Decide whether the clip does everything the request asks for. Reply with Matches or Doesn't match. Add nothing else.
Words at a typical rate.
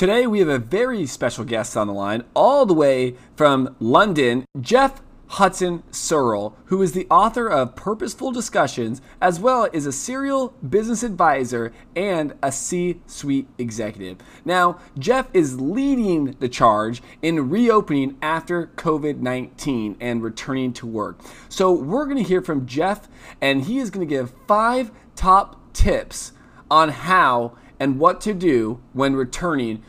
Matches